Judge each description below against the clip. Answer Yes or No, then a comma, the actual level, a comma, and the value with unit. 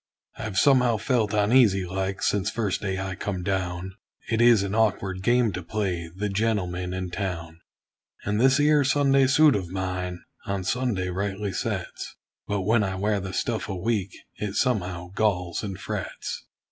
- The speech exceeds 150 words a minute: Yes, average, 165 wpm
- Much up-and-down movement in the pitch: No, average, 3.3 semitones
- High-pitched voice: No, low, 100 Hz